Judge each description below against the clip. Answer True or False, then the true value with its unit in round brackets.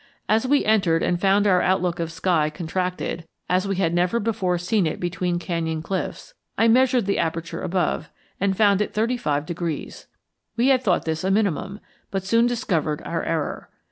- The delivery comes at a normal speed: True (180 wpm)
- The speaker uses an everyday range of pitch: True (3.9 semitones)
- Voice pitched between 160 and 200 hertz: True (185 Hz)